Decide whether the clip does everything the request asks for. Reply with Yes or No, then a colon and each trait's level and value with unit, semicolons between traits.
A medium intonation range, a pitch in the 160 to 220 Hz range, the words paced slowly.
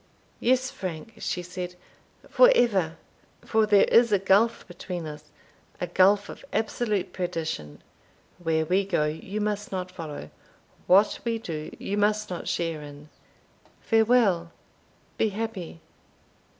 Yes: average, 4.3 semitones; high, 190 Hz; slow, 125 wpm